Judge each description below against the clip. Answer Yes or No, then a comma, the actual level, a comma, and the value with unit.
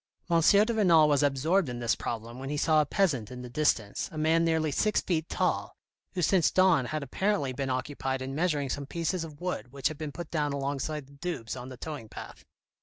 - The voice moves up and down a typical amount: Yes, average, 3.9 semitones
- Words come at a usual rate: No, fast, 220 wpm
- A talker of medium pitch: Yes, medium, 150 Hz